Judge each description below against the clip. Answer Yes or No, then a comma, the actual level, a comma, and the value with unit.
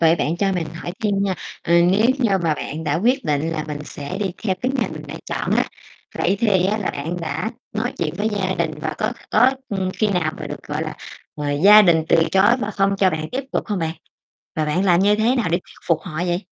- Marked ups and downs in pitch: No, average, 4.3 semitones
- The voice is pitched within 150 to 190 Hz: Yes, medium, 185 Hz